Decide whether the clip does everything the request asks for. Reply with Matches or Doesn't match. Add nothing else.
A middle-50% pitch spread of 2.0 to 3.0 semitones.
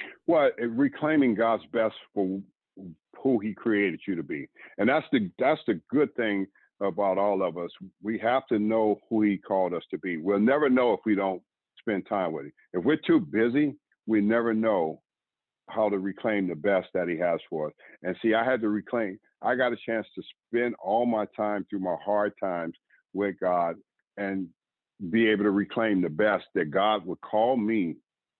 Matches